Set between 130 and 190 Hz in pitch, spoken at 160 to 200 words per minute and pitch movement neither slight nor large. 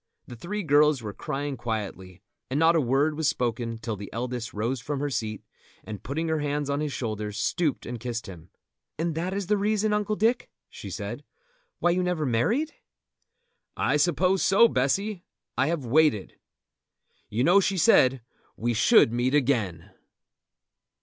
No: medium, 140 Hz; average, 165 wpm; wide, 6.7 semitones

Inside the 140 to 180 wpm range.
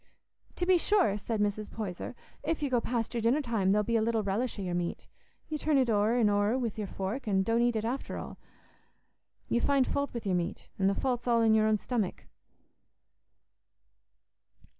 No: average, 200 wpm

